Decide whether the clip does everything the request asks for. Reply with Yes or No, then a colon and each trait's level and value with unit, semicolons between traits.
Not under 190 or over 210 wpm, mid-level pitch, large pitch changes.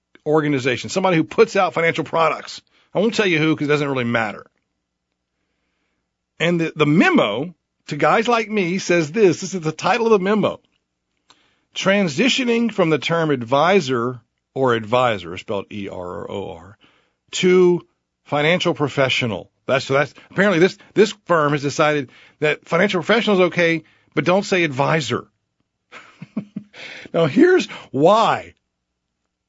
No: slow, 135 wpm; medium, 155 Hz; wide, 6.8 semitones